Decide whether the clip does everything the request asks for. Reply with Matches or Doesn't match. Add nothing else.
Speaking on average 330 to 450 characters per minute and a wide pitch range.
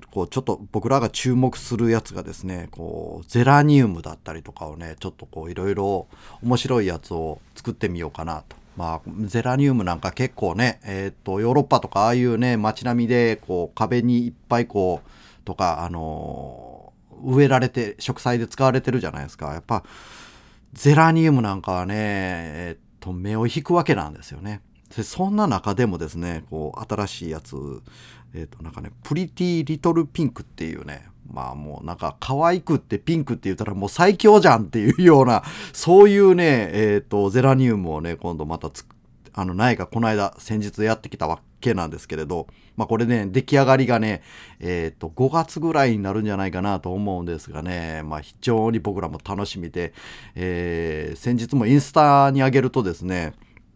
Matches